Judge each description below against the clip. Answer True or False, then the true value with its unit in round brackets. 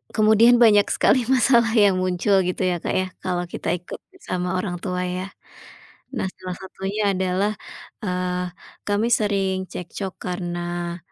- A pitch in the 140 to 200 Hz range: True (185 Hz)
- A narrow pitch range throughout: True (2.3 semitones)